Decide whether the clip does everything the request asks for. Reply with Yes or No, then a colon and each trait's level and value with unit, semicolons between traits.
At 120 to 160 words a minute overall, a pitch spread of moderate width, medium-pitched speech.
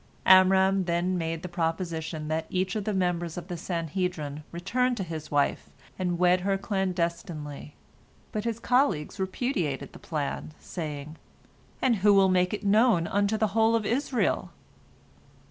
Yes: average, 150 wpm; average, 3.5 semitones; medium, 180 Hz